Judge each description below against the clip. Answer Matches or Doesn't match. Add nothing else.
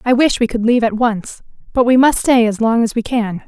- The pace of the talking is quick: Matches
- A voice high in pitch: Matches